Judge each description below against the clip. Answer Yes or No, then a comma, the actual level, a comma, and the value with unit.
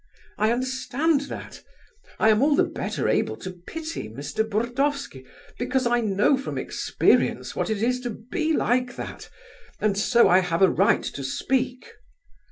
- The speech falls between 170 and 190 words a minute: No, average, 160 wpm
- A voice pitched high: Yes, high, 240 Hz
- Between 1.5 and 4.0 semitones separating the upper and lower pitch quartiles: No, average, 4.5 semitones